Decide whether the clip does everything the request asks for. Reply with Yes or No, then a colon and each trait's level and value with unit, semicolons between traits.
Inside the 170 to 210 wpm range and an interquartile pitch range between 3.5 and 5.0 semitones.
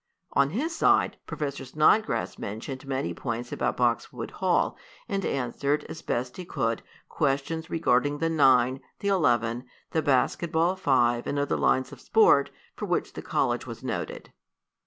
No: average, 155 wpm; average, 4.6 semitones